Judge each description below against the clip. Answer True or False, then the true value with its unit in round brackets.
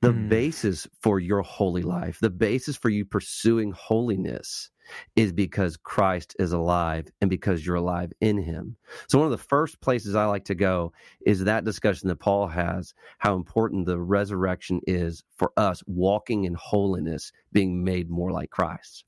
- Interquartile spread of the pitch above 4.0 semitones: False (3.2 semitones)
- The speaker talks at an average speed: True (170 wpm)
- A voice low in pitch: True (100 Hz)